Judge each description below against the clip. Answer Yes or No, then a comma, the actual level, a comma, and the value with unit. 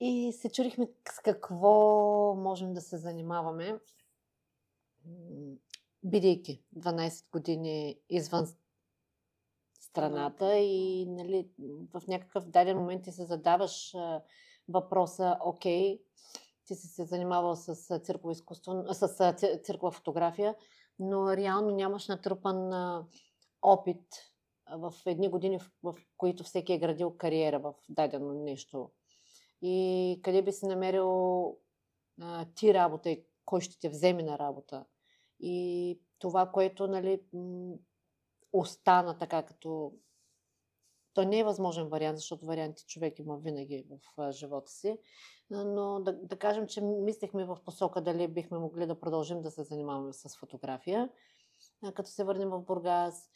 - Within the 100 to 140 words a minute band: Yes, average, 125 wpm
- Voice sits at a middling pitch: Yes, medium, 180 Hz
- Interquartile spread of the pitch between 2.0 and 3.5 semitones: Yes, average, 2.8 semitones